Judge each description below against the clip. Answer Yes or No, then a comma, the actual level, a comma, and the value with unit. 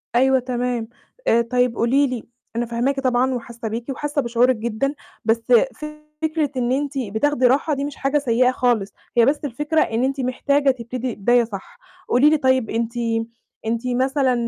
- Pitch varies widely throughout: No, average, 2.7 semitones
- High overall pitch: Yes, very high, 250 Hz